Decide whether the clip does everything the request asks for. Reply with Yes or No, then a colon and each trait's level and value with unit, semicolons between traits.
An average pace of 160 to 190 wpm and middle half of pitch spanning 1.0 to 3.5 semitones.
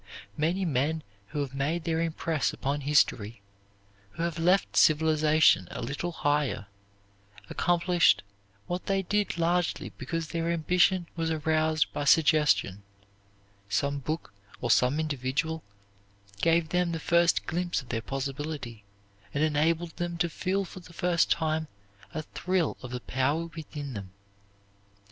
No: slow, 135 wpm; average, 3.0 semitones